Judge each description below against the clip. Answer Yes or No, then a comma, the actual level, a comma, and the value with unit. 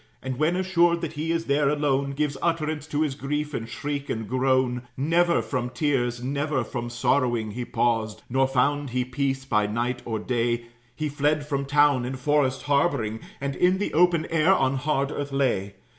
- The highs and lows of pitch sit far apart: No, average, 3.2 semitones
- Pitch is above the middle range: No, medium, 140 Hz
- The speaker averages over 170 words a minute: Yes, average, 185 wpm